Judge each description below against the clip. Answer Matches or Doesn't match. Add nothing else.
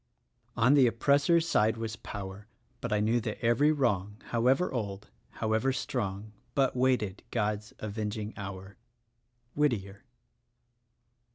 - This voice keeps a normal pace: Doesn't match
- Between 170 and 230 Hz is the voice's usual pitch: Doesn't match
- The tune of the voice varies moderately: Matches